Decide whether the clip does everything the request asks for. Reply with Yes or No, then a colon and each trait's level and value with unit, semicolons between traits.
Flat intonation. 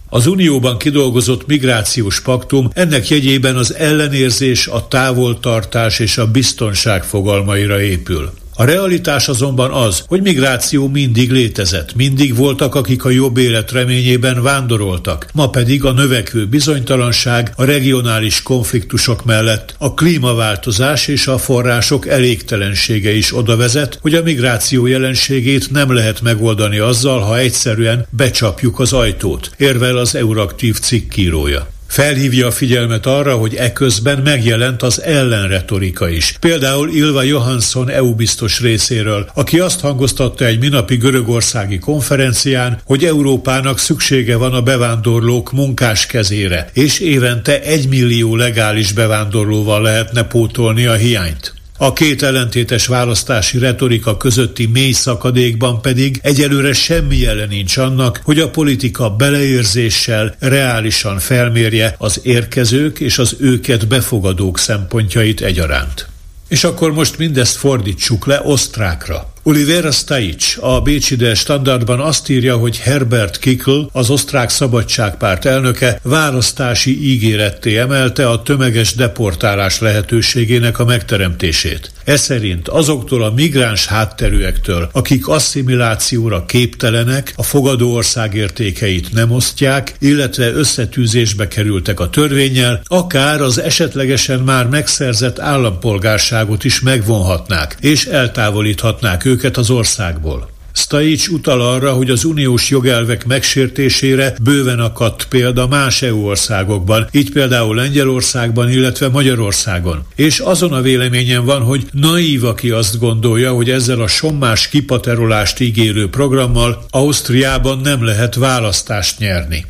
No: average, 3.2 semitones